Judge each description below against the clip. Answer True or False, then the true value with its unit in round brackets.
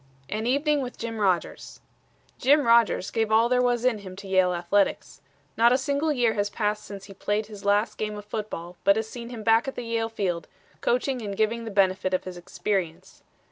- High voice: True (215 Hz)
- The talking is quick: True (210 wpm)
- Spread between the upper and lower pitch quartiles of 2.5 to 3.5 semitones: True (3.1 semitones)